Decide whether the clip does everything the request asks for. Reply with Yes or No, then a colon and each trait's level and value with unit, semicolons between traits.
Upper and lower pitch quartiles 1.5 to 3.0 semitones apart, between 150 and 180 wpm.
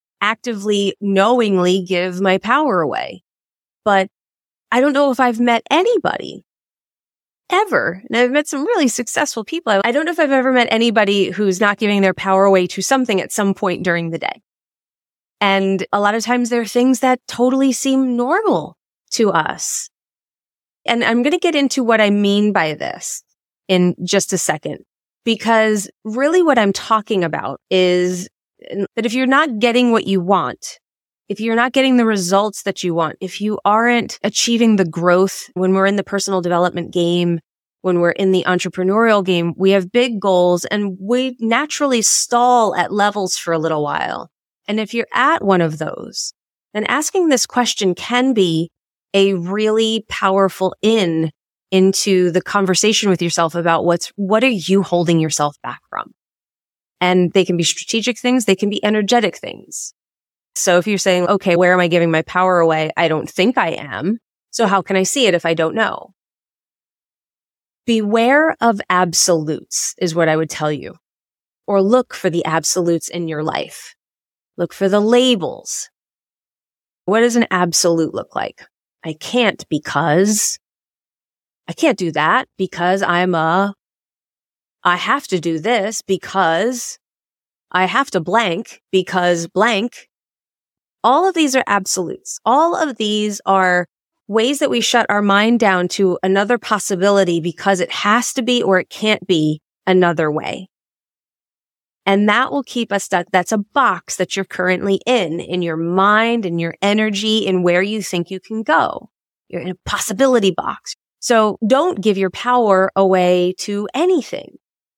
No: average, 4.4 semitones; average, 165 wpm